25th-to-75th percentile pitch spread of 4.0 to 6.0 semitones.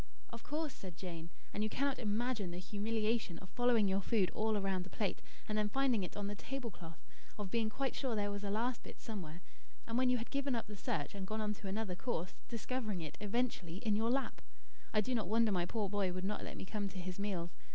No: average, 3.5 semitones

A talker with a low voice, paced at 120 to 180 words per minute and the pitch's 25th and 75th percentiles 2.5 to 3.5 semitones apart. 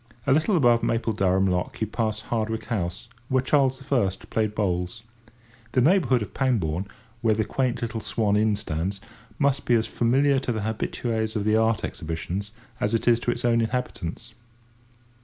Yes: low, 110 Hz; average, 170 wpm; average, 3.2 semitones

